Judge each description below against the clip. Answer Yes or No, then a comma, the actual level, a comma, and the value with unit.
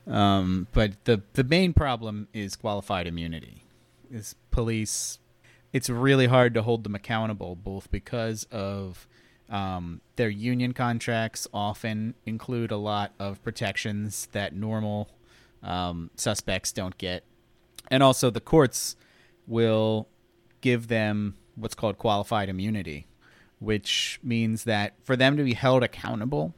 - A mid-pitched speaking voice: No, low, 110 Hz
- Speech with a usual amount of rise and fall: Yes, average, 3.0 semitones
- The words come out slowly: Yes, slow, 130 wpm